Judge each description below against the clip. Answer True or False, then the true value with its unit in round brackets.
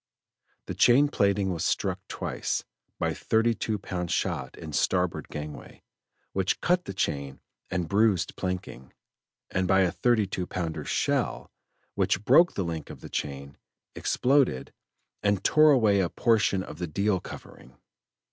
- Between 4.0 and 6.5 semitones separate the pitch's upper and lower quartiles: True (4.6 semitones)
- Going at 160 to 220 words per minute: False (150 wpm)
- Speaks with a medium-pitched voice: False (95 Hz)